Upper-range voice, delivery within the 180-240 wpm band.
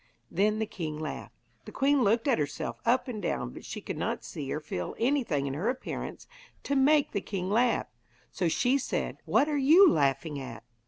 Yes: high, 210 Hz; average, 200 wpm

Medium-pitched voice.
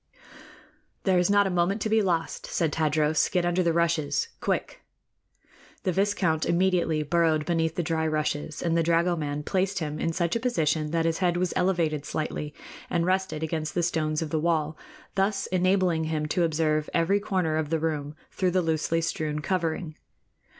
Yes: medium, 165 Hz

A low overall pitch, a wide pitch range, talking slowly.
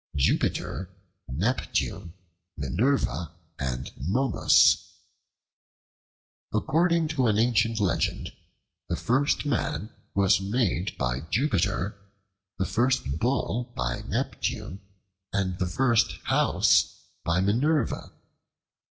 Yes: low, 100 Hz; wide, 6.6 semitones; slow, 90 wpm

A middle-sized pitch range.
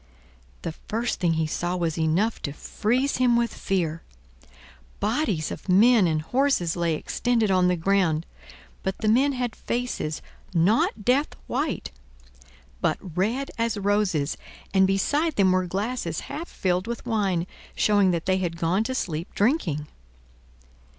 No: wide, 5.7 semitones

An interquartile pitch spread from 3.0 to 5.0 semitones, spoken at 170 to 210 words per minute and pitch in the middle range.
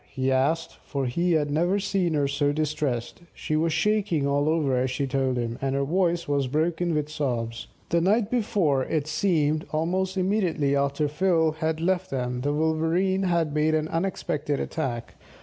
Yes: average, 3.6 semitones; average, 175 wpm; medium, 155 Hz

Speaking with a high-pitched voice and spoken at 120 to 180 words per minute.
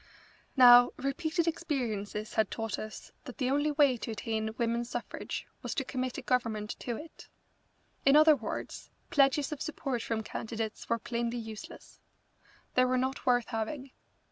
Yes: high, 245 Hz; average, 155 wpm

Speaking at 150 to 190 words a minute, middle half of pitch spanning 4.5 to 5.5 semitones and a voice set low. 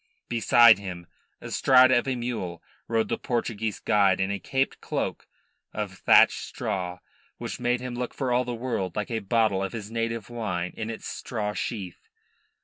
No: average, 170 wpm; average, 3.7 semitones; low, 115 Hz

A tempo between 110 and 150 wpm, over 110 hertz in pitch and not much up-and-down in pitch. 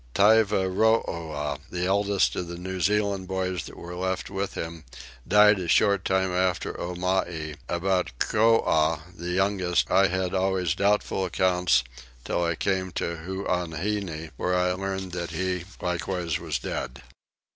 No: average, 140 wpm; very low, 90 Hz; narrow, 1.9 semitones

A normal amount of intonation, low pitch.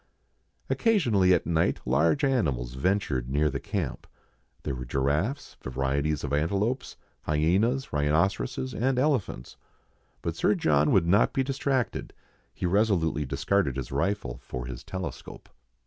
No: wide, 7.8 semitones; very low, 85 Hz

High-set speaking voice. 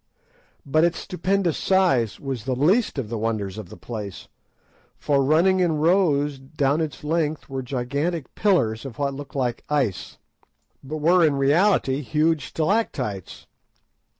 No: medium, 145 Hz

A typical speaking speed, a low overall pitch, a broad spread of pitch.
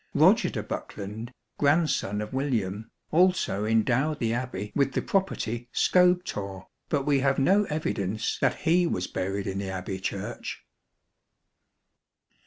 No: slow, 130 wpm; low, 120 Hz; wide, 6.9 semitones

